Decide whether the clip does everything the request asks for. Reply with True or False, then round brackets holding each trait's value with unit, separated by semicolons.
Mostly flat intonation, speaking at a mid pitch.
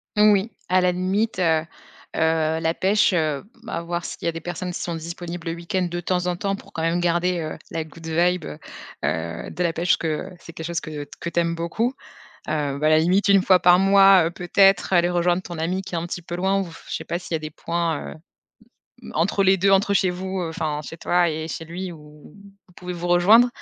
True (2.3 semitones; 175 Hz)